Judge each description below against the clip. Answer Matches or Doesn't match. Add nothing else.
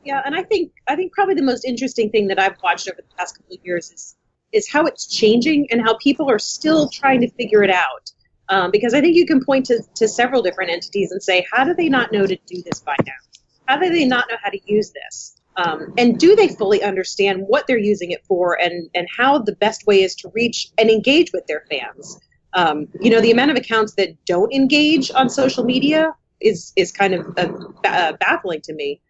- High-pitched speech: Matches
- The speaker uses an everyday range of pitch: Doesn't match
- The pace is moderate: Doesn't match